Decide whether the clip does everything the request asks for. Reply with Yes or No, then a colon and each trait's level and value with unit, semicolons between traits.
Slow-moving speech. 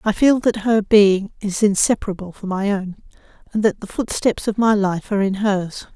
No: average, 200 wpm